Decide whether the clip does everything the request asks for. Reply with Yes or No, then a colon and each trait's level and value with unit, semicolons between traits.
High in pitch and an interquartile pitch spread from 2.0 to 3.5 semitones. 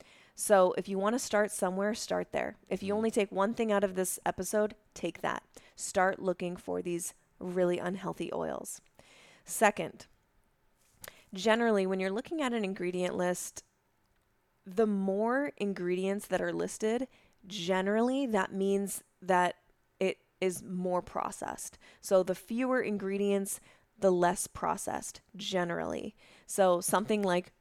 Yes: high, 195 Hz; narrow, 2.5 semitones